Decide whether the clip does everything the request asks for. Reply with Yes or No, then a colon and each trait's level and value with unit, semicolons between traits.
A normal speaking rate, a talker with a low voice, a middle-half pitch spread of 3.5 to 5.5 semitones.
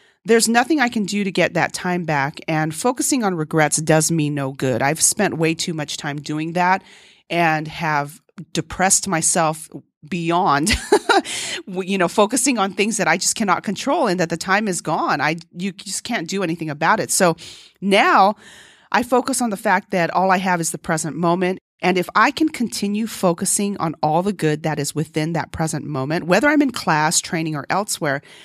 No: average, 195 wpm; medium, 175 Hz; average, 4.0 semitones